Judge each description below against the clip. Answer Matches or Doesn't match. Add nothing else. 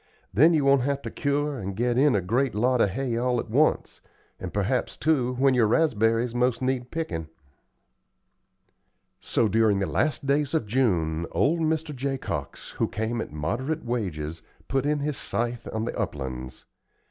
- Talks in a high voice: Doesn't match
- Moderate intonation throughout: Matches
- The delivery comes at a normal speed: Matches